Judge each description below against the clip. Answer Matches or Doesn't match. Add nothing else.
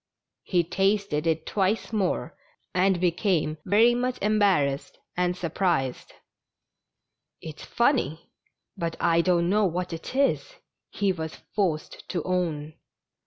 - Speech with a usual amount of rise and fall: Matches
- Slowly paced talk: Matches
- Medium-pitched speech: Matches